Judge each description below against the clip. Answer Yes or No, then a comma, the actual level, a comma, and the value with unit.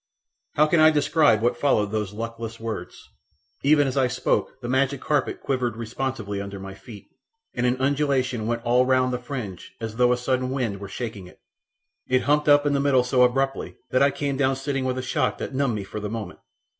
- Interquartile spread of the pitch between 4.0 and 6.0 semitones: No, average, 3.3 semitones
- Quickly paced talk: Yes, fast, 210 wpm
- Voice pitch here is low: Yes, low, 125 Hz